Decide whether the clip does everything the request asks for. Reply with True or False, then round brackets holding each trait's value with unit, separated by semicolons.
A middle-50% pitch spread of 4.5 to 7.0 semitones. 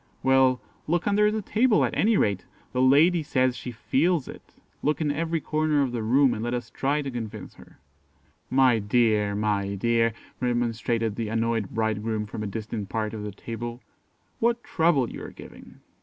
True (5.1 semitones)